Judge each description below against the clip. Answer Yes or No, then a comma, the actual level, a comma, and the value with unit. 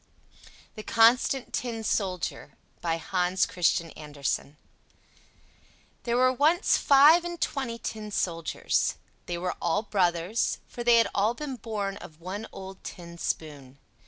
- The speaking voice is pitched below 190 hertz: No, high, 200 Hz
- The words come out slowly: Yes, slow, 130 wpm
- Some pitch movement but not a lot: No, wide, 5.8 semitones